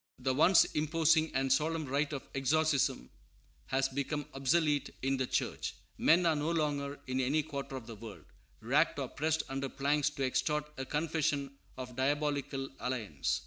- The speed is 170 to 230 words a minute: No, average, 160 wpm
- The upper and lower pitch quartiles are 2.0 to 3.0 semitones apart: Yes, narrow, 2.5 semitones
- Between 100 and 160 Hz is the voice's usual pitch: Yes, medium, 140 Hz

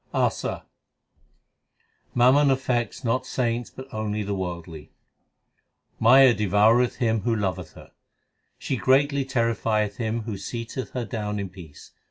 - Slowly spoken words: Yes, slow, 125 wpm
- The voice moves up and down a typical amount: Yes, average, 3.4 semitones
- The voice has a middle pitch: No, low, 115 Hz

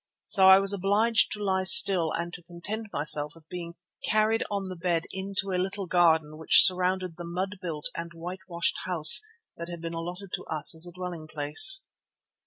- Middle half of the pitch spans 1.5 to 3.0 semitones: Yes, narrow, 2.5 semitones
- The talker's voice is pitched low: No, medium, 180 Hz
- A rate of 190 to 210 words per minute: Yes, average, 195 wpm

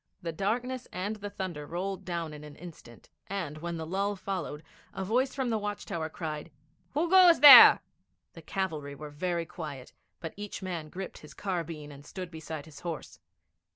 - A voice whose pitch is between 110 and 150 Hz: No, medium, 175 Hz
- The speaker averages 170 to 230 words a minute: Yes, average, 180 wpm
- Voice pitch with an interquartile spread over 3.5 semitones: Yes, average, 4.4 semitones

